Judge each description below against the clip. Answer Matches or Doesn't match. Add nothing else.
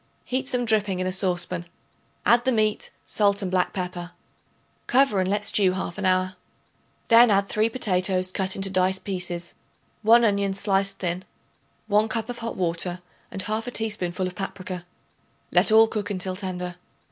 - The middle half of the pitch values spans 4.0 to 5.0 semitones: Doesn't match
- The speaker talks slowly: Doesn't match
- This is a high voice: Matches